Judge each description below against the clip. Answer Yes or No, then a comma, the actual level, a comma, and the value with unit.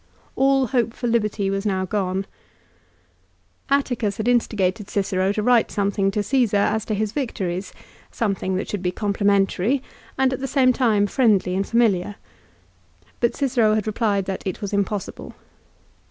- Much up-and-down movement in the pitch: No, average, 3.4 semitones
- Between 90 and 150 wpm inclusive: No, average, 165 wpm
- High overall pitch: Yes, high, 210 Hz